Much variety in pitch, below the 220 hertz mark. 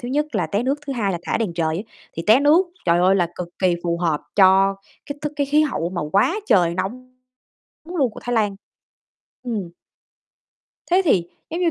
Yes: wide, 8.0 semitones; high, 210 Hz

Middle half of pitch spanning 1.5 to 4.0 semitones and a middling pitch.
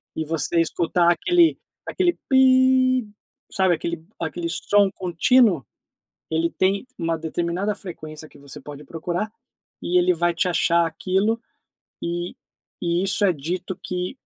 Yes: average, 3.5 semitones; medium, 175 Hz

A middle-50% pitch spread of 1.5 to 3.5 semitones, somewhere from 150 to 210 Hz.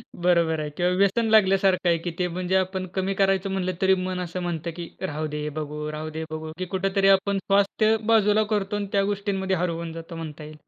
Yes: narrow, 2.6 semitones; medium, 185 Hz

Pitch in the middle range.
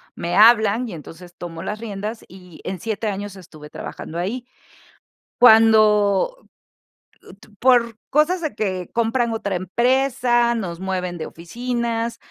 No: high, 215 Hz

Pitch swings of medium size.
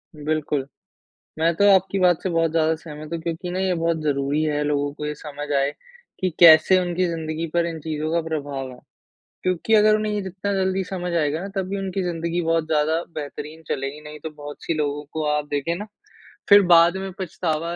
Yes: average, 3.3 semitones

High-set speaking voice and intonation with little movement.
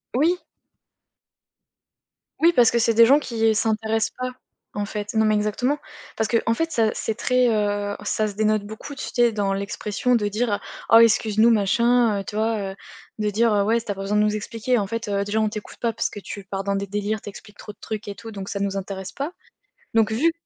Yes: high, 215 Hz; narrow, 2.1 semitones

